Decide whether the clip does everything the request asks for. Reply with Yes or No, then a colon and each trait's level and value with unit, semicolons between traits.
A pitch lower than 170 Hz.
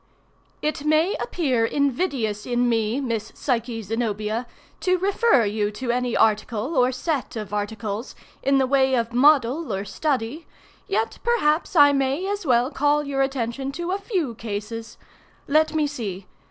No: very high, 255 Hz